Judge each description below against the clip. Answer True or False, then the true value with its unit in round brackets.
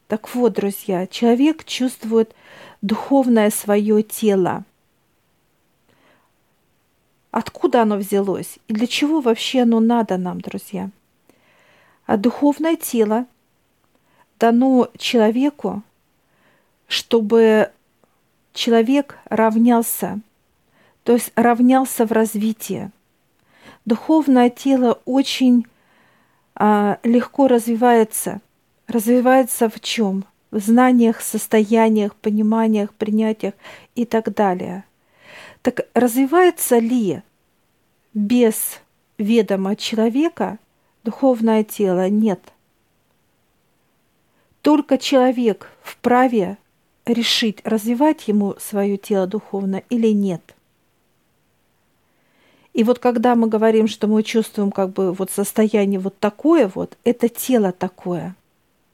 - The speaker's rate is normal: False (90 wpm)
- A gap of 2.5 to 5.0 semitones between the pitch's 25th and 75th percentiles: True (2.8 semitones)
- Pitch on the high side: True (225 Hz)